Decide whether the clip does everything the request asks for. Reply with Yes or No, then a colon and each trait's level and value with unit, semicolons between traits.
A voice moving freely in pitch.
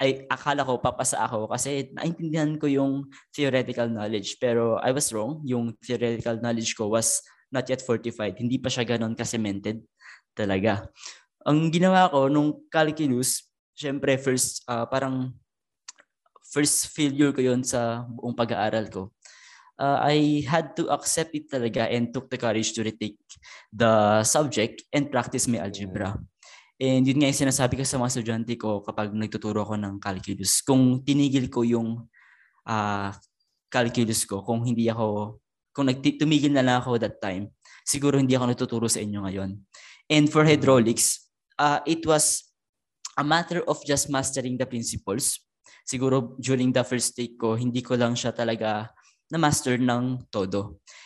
No: average, 3.6 semitones